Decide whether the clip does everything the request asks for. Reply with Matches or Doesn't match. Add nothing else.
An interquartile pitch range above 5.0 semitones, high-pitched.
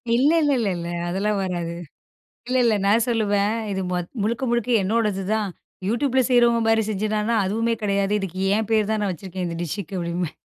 Doesn't match